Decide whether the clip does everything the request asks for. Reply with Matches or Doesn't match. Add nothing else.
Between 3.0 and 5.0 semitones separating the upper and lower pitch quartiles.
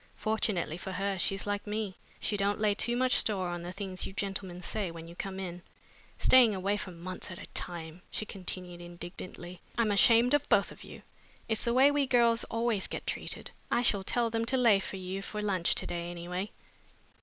Matches